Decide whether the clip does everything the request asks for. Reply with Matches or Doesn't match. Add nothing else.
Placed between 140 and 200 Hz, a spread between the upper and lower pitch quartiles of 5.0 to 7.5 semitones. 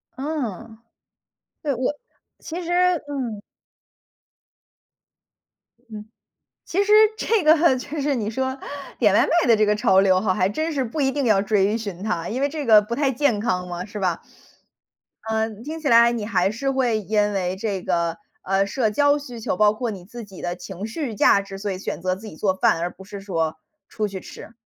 Doesn't match